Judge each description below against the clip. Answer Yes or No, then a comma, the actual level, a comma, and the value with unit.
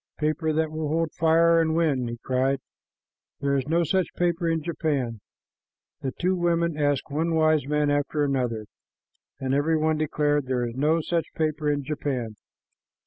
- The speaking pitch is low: No, medium, 150 Hz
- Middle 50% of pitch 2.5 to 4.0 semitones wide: Yes, average, 2.8 semitones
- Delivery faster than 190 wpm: No, average, 165 wpm